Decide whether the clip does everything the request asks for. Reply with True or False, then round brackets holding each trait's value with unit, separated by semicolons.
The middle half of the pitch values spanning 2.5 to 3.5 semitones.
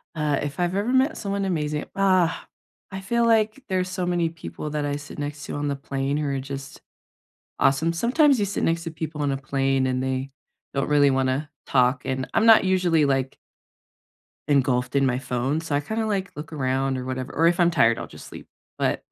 False (5.2 semitones)